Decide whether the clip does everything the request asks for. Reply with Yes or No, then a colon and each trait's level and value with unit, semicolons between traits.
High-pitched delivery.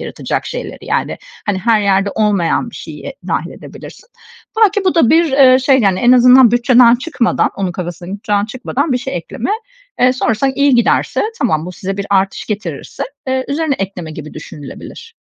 Yes: high, 235 Hz